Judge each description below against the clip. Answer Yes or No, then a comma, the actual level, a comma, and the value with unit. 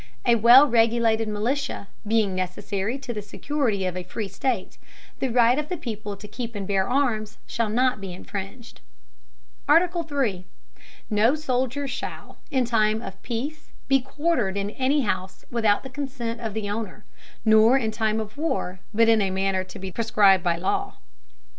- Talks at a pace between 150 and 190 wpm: Yes, average, 165 wpm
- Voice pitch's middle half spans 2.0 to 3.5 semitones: No, average, 4.3 semitones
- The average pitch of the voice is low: No, high, 225 Hz